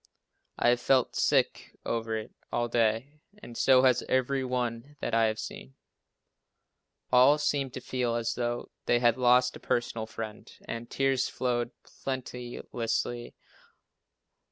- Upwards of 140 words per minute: No, slow, 135 wpm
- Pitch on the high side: No, low, 120 Hz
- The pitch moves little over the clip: Yes, narrow, 1.7 semitones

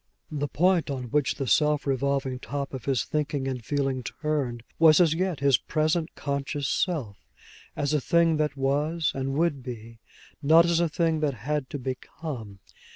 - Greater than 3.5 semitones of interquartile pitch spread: No, average, 2.9 semitones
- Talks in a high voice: No, medium, 145 Hz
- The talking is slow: No, average, 170 wpm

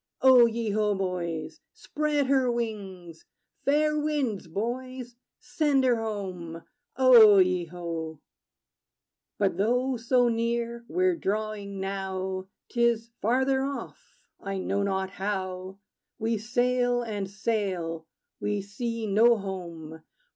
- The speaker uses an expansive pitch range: No, average, 4.4 semitones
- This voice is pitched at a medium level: No, high, 215 Hz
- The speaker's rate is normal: No, slow, 115 wpm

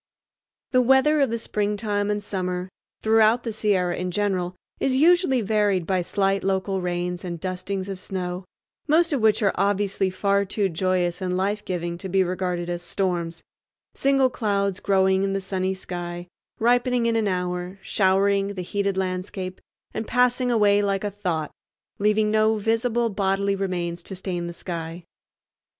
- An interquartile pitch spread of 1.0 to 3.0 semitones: Yes, average, 2.7 semitones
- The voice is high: Yes, high, 195 Hz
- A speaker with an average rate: Yes, average, 160 wpm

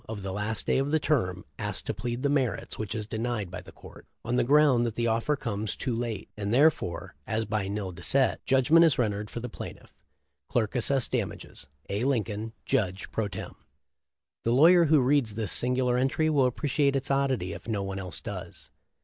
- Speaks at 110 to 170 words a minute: No, fast, 205 wpm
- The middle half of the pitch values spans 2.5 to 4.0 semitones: No, average, 4.5 semitones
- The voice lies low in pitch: Yes, low, 115 Hz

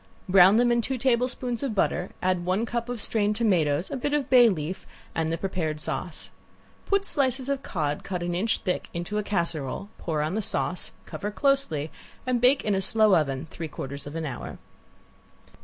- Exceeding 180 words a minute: Yes, average, 190 wpm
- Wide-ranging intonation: Yes, wide, 6.6 semitones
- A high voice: Yes, high, 195 Hz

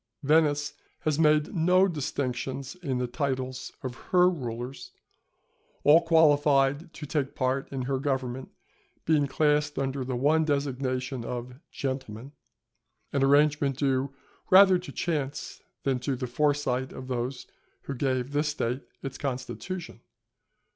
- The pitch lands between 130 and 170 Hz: Yes, medium, 140 Hz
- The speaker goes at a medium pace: No, slow, 130 wpm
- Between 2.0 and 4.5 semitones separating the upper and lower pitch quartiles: Yes, narrow, 2.6 semitones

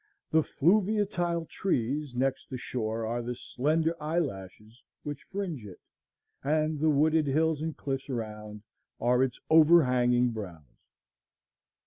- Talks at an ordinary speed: No, slow, 120 wpm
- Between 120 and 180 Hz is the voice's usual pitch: Yes, medium, 140 Hz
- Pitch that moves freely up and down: No, average, 5.0 semitones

